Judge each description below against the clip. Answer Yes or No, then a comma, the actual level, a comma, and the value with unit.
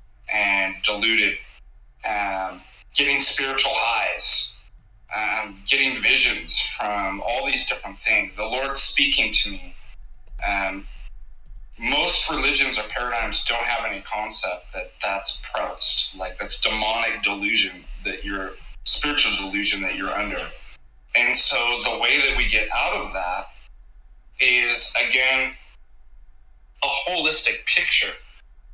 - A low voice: Yes, low, 105 Hz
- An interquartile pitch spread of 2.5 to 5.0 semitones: No, wide, 5.4 semitones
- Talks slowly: Yes, slow, 120 wpm